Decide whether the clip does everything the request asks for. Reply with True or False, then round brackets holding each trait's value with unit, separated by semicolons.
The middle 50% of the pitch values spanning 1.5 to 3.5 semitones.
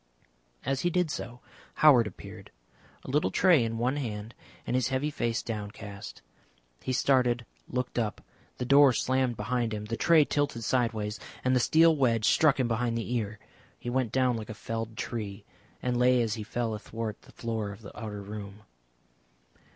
True (3.1 semitones)